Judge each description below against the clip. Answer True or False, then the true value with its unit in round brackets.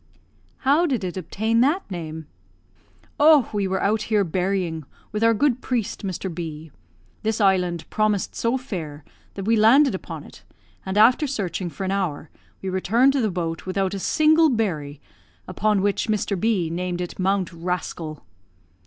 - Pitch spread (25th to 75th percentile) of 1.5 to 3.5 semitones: False (4.3 semitones)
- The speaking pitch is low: False (195 Hz)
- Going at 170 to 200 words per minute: False (160 wpm)